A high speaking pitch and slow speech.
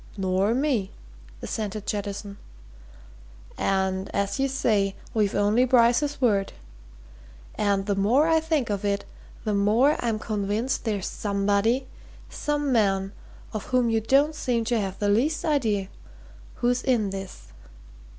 Yes: high, 215 Hz; slow, 130 wpm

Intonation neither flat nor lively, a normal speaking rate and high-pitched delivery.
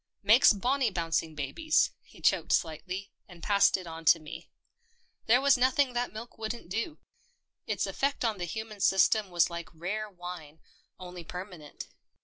Yes: average, 5.0 semitones; average, 160 wpm; high, 195 Hz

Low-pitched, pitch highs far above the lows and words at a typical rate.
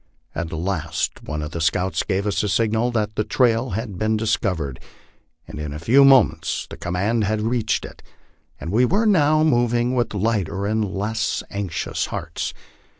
No: low, 105 Hz; average, 4.8 semitones; average, 165 wpm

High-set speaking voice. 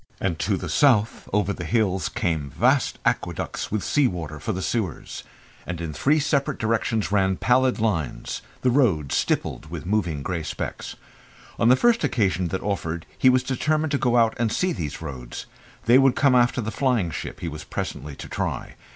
No: low, 105 Hz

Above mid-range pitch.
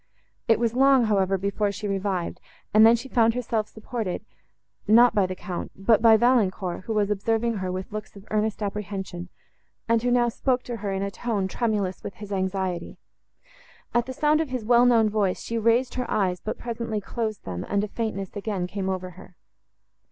Yes: high, 215 Hz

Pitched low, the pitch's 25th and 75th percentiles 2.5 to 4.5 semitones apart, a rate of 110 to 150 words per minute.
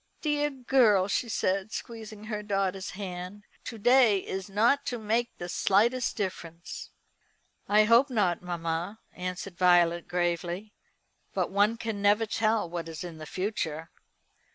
No: high, 200 Hz; average, 4.0 semitones; average, 140 wpm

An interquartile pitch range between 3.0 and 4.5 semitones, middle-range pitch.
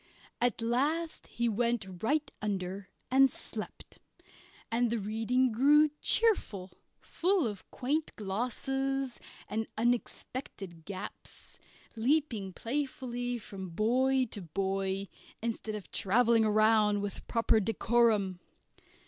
No: average, 4.2 semitones; high, 230 Hz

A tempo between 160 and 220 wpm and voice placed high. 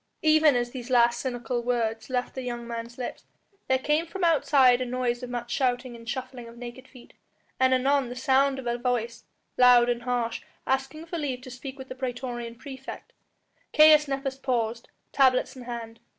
Yes: average, 185 wpm; very high, 250 Hz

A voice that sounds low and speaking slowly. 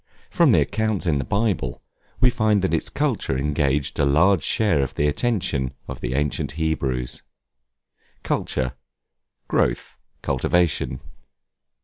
Yes: very low, 75 Hz; slow, 125 wpm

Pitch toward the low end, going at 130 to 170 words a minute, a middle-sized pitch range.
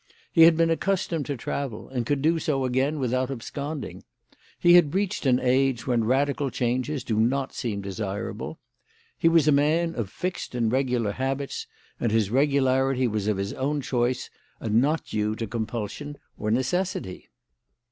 Yes: low, 130 Hz; average, 165 wpm; average, 4.0 semitones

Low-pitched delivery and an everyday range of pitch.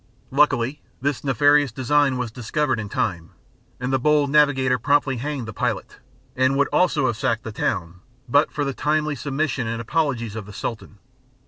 Yes: low, 130 Hz; average, 4.0 semitones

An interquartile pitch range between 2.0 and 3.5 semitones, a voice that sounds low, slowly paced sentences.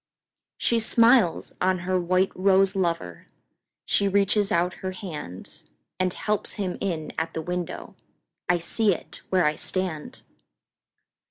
No: narrow, 2.6 semitones; medium, 185 Hz; slow, 115 wpm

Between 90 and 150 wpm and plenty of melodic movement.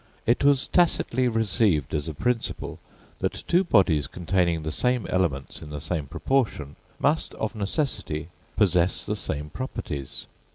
Yes: average, 140 wpm; wide, 8.4 semitones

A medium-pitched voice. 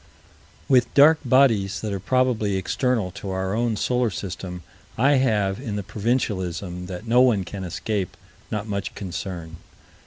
No: low, 105 Hz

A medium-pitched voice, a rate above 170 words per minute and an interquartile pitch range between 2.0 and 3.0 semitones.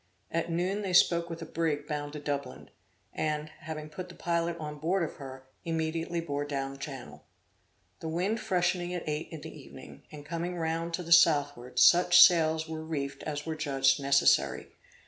Yes: medium, 160 Hz; average, 180 wpm; average, 2.7 semitones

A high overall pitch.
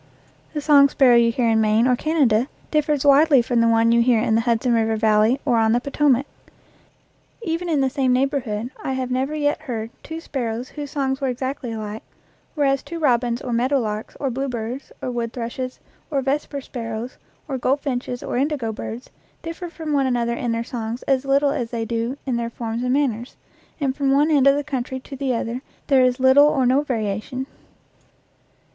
Yes: very high, 255 Hz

